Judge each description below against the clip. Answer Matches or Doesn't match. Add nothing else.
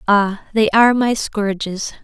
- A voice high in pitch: Matches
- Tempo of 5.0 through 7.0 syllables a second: Doesn't match